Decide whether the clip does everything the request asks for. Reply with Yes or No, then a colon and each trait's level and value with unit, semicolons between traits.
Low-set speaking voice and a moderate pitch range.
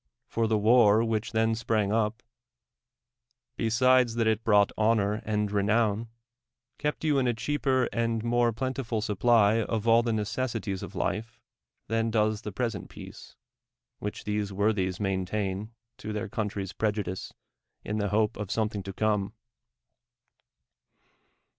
No: low, 110 Hz; narrow, 2.0 semitones